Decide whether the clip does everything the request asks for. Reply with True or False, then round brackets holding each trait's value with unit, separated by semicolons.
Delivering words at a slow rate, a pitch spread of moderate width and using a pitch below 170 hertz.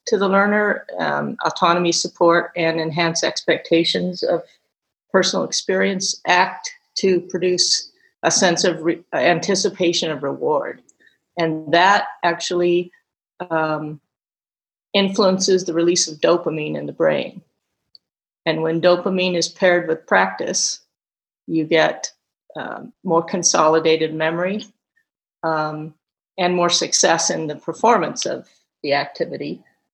False (115 wpm; 3.0 semitones; 175 Hz)